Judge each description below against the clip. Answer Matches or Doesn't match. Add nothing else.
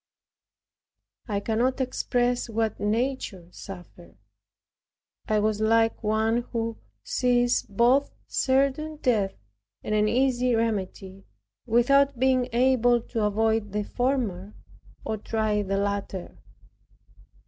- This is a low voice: Doesn't match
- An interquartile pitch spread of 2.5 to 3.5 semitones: Matches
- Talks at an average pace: Doesn't match